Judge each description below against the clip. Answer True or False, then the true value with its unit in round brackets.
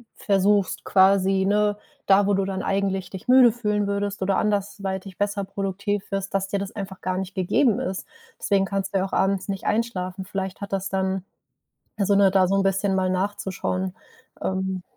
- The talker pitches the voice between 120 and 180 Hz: False (195 Hz)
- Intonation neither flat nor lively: False (1.1 semitones)